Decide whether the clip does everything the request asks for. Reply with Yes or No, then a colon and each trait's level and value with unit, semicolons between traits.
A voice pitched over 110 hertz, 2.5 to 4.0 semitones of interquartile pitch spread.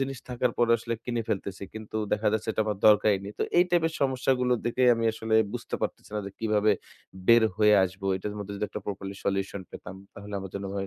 No: low, 105 Hz; average, 2.9 semitones